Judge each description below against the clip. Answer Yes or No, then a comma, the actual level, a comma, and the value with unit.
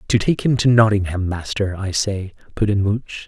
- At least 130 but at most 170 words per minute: No, average, 200 wpm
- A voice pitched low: Yes, low, 105 Hz